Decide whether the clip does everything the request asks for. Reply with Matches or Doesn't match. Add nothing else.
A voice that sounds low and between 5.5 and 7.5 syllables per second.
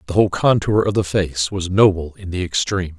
Matches